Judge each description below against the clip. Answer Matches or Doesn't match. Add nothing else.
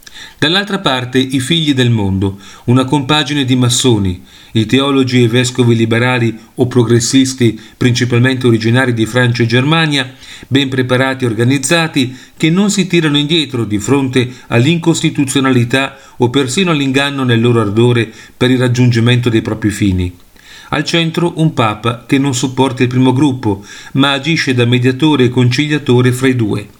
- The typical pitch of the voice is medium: Doesn't match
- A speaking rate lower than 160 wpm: Matches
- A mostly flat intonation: Doesn't match